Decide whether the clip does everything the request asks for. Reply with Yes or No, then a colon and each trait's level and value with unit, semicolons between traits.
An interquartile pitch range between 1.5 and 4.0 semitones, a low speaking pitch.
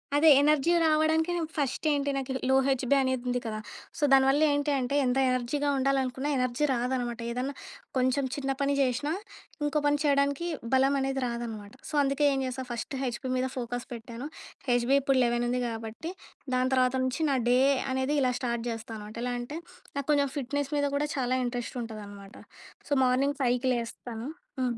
No: narrow, 2.6 semitones; very high, 260 Hz